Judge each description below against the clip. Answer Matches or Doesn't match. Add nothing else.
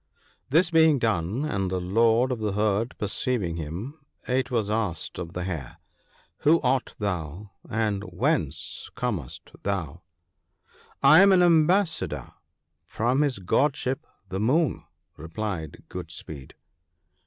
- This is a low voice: Matches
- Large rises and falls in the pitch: Matches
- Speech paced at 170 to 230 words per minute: Doesn't match